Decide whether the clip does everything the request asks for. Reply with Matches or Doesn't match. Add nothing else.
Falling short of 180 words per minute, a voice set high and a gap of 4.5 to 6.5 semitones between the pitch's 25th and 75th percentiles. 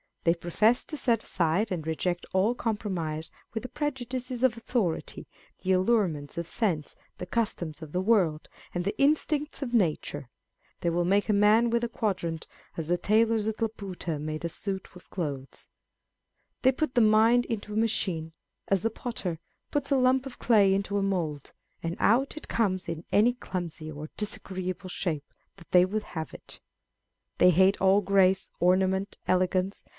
Matches